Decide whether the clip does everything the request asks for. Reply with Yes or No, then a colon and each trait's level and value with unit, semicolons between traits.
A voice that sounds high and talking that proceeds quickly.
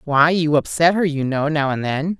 No: medium, 155 Hz; fast, 245 wpm